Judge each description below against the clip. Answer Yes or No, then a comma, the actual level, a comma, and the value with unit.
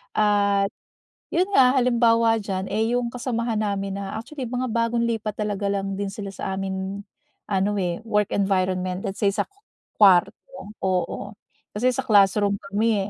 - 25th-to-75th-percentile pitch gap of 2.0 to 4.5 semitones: Yes, average, 2.8 semitones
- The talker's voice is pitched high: Yes, high, 205 Hz